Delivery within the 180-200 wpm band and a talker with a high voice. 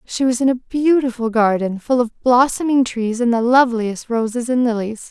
Yes: average, 190 wpm; high, 240 Hz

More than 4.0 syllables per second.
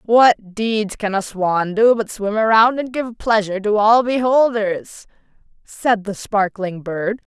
No: 3.8 syllables/s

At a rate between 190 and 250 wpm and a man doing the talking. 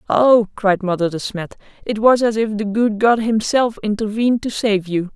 No: average, 200 wpm; female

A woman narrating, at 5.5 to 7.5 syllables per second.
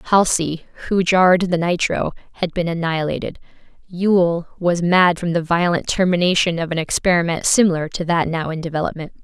Yes: female; 5.6 syllables/s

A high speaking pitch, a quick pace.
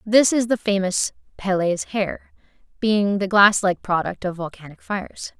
No: high, 195 Hz; average, 155 wpm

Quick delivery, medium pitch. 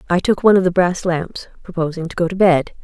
Yes: fast, 255 wpm; medium, 175 Hz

